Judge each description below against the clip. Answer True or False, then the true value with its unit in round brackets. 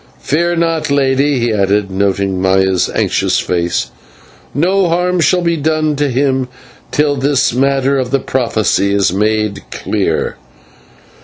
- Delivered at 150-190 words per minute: False (135 wpm)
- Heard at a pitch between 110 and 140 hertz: True (135 Hz)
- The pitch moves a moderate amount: False (7.0 semitones)